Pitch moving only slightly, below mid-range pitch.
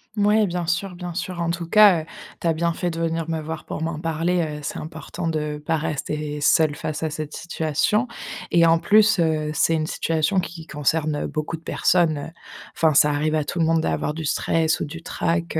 No: narrow, 1.7 semitones; medium, 160 Hz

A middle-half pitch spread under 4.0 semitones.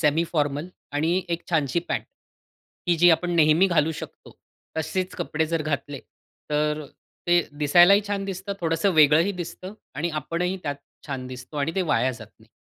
Yes: average, 3.1 semitones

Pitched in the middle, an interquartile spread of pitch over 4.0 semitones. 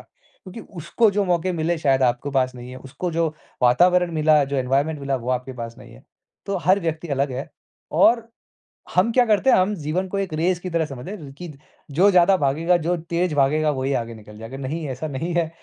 Yes: medium, 160 Hz; average, 5.1 semitones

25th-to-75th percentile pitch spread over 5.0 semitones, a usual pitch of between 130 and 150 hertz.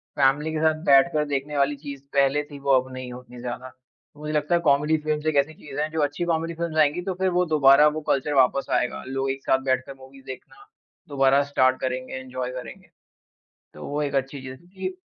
No: narrow, 2.6 semitones; medium, 140 Hz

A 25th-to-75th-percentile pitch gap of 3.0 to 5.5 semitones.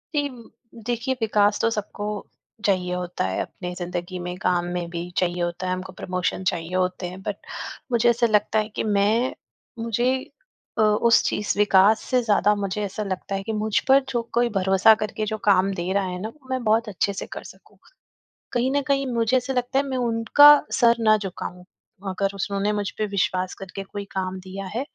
Yes: average, 3.6 semitones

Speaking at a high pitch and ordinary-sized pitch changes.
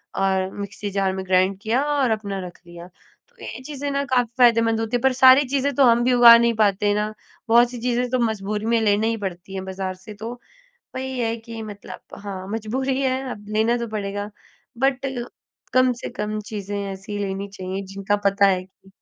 Yes: high, 215 Hz; average, 3.8 semitones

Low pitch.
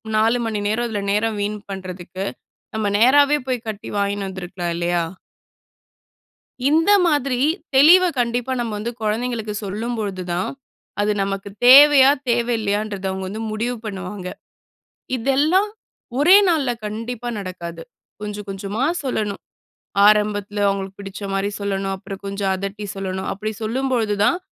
No: high, 210 Hz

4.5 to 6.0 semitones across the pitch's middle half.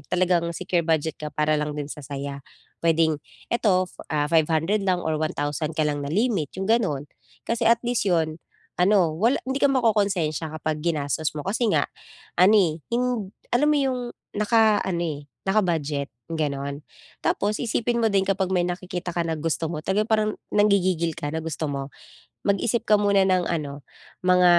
Yes: average, 5.2 semitones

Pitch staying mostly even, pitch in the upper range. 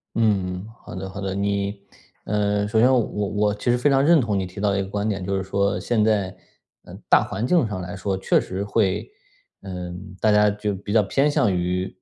No: narrow, 1.9 semitones; low, 100 Hz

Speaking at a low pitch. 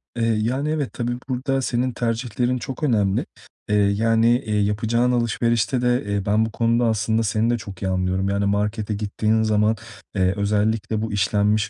Yes: low, 110 Hz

